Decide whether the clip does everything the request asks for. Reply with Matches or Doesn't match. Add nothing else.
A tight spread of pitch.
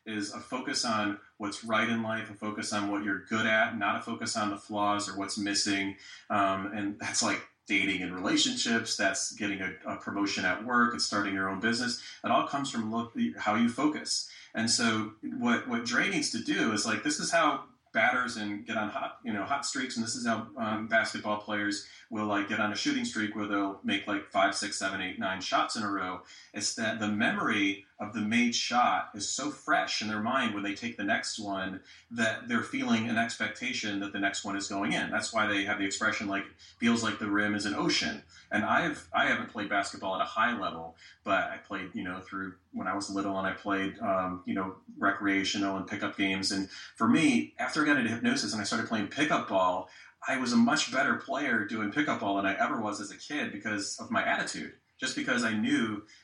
Matches